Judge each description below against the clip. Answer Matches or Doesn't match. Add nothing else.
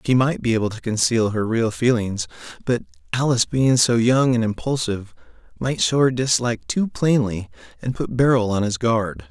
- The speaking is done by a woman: Doesn't match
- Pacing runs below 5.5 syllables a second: Matches